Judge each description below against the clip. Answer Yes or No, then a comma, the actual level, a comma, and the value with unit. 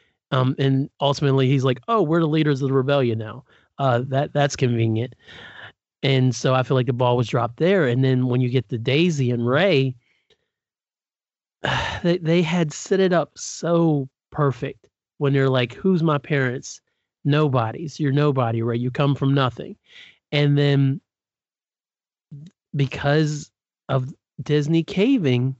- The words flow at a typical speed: Yes, average, 150 wpm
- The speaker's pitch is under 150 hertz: Yes, medium, 140 Hz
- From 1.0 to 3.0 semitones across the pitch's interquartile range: Yes, average, 2.7 semitones